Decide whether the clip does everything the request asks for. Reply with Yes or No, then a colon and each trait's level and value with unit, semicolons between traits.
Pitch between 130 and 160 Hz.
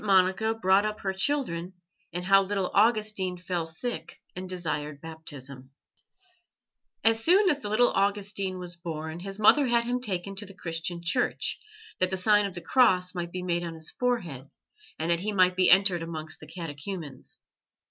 No: medium, 185 Hz